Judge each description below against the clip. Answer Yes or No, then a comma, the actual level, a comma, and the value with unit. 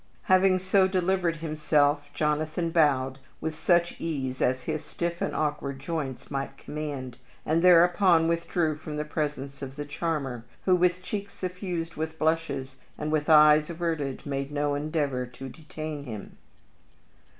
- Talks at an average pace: Yes, average, 145 wpm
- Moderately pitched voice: Yes, medium, 155 Hz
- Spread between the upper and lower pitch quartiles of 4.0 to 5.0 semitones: No, average, 2.9 semitones